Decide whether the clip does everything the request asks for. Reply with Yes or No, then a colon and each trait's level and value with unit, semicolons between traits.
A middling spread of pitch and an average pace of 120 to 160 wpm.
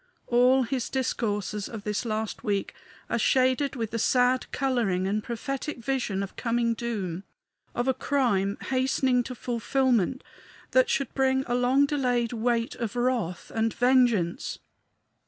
Yes: average, 3.1 semitones; average, 140 wpm